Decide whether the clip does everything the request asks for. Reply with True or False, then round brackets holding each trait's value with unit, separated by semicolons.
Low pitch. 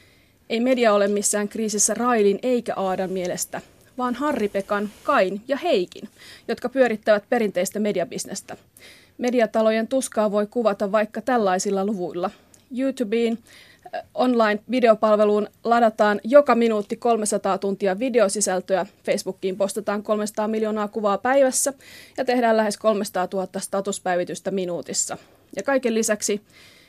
False (215 Hz)